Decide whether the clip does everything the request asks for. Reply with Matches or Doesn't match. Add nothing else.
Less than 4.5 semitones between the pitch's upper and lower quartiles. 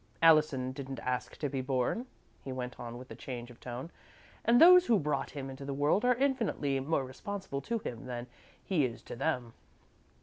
Doesn't match